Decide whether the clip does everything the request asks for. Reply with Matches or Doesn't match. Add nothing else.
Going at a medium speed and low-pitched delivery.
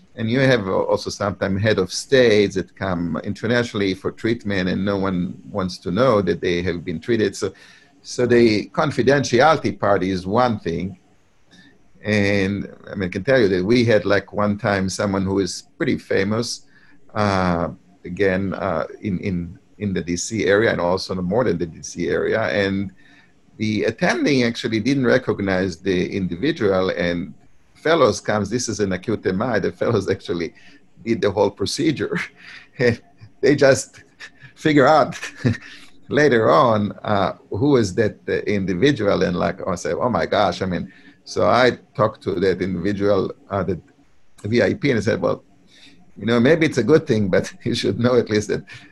Matches